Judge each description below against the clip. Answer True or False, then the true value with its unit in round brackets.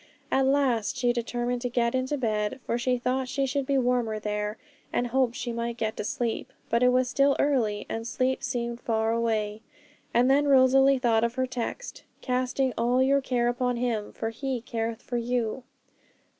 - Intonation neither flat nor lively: False (2.1 semitones)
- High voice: True (245 Hz)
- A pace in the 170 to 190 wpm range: True (185 wpm)